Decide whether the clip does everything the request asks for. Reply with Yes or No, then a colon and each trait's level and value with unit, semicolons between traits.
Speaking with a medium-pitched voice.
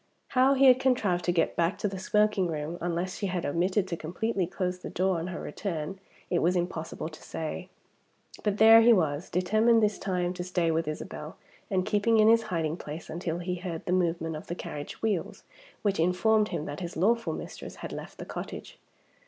Yes: medium, 180 Hz